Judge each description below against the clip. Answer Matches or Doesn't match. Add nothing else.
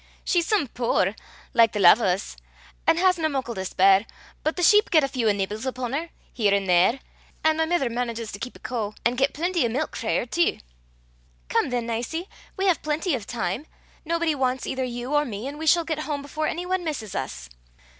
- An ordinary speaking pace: Doesn't match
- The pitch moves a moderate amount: Doesn't match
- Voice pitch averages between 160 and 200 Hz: Doesn't match